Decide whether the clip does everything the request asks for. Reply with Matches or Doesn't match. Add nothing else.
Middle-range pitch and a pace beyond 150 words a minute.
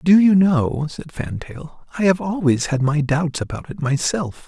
Matches